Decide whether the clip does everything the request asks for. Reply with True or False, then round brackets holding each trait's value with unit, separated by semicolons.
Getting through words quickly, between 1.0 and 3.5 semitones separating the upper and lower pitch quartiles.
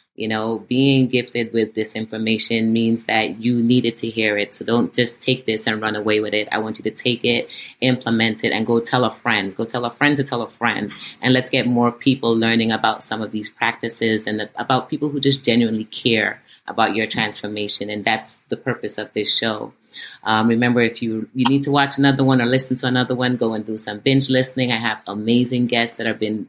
True (230 wpm; 2.5 semitones)